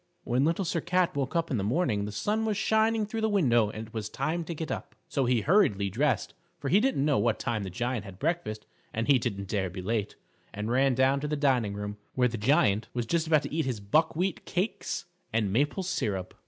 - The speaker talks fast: Yes, fast, 235 wpm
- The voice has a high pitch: No, low, 130 Hz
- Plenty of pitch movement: Yes, wide, 7.6 semitones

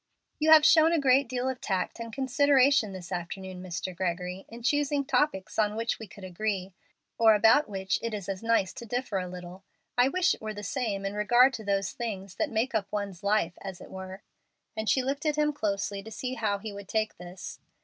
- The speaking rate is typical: No, fast, 220 wpm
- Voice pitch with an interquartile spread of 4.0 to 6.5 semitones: Yes, average, 4.8 semitones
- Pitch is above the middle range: Yes, high, 215 Hz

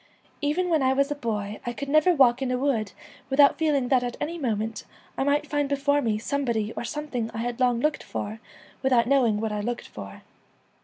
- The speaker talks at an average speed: No, fast, 210 wpm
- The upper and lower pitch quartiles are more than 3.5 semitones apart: Yes, average, 3.9 semitones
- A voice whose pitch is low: No, very high, 255 Hz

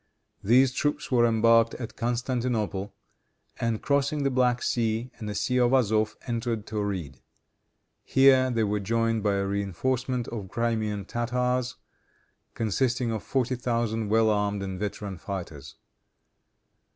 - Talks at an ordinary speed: No, slow, 130 wpm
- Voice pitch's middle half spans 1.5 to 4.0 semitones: Yes, average, 3.3 semitones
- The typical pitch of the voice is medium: No, low, 115 Hz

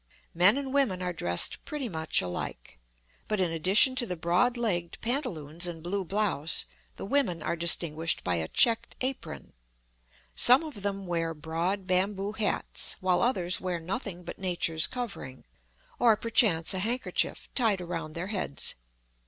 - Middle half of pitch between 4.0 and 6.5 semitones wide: Yes, average, 5.0 semitones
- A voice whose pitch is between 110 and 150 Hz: No, medium, 185 Hz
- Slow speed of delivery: No, average, 155 wpm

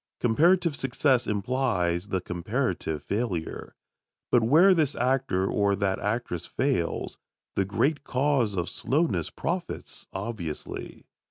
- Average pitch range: No, wide, 6.3 semitones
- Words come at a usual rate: No, slow, 110 wpm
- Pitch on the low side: Yes, low, 115 Hz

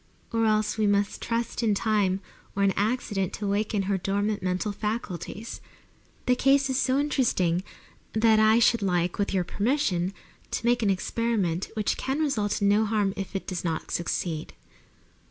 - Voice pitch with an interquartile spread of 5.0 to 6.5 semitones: No, average, 3.0 semitones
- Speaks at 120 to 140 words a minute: No, average, 170 wpm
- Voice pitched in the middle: No, high, 210 Hz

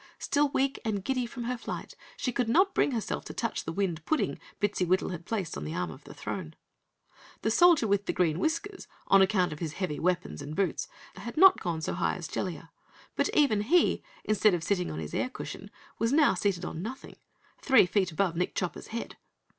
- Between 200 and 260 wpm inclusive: Yes, fast, 205 wpm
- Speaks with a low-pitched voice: No, high, 195 Hz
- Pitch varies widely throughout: Yes, wide, 6.1 semitones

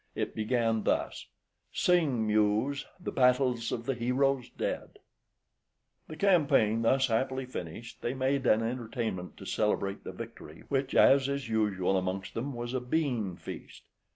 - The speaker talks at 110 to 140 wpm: No, average, 150 wpm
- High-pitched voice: No, low, 120 Hz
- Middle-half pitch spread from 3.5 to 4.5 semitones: Yes, average, 3.8 semitones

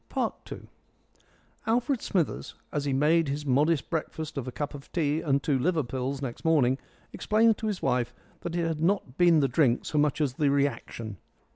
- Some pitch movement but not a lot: Yes, average, 3.7 semitones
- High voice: No, medium, 150 Hz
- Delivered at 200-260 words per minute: No, average, 185 wpm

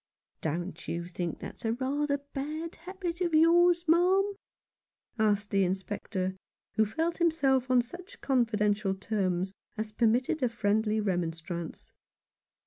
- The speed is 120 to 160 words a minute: Yes, slow, 135 wpm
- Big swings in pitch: Yes, wide, 8.5 semitones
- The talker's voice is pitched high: Yes, high, 225 Hz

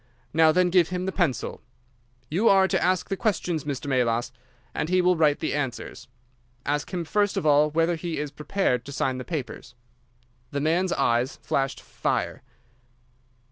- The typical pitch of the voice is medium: Yes, medium, 155 Hz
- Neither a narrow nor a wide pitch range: Yes, average, 4.3 semitones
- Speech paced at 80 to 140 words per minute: No, average, 170 wpm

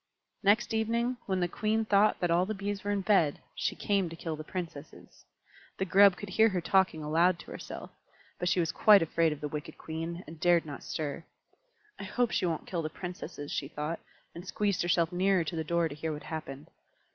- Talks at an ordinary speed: No, fast, 215 wpm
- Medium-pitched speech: Yes, medium, 175 Hz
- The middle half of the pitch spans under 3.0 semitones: No, average, 3.7 semitones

